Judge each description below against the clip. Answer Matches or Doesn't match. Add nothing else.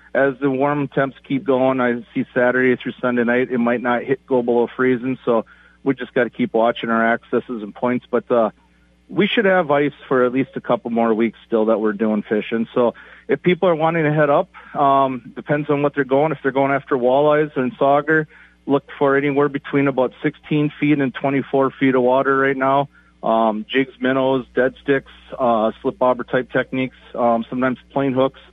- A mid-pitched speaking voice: Doesn't match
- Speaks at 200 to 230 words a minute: Matches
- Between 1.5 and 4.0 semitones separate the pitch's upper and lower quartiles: Matches